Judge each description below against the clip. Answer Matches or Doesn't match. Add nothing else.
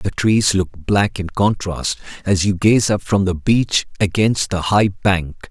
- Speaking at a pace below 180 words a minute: Doesn't match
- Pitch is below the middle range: Matches